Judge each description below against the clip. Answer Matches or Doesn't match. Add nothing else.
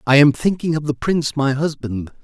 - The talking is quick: Matches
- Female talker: Doesn't match